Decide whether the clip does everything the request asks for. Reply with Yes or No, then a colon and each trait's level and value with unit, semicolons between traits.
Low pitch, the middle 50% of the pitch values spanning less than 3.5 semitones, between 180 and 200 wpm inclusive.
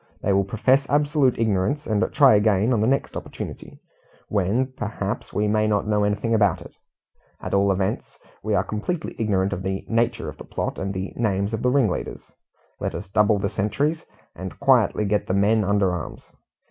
Yes: low, 105 Hz; average, 3.0 semitones; average, 185 wpm